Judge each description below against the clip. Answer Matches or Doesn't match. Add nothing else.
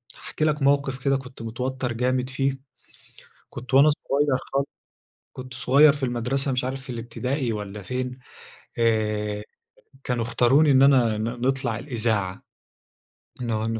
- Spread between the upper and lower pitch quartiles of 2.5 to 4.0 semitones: Matches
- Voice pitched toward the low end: Matches